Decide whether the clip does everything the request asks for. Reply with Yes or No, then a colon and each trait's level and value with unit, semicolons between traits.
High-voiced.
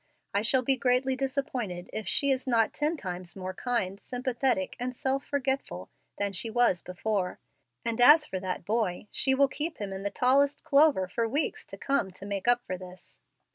Yes: high, 235 Hz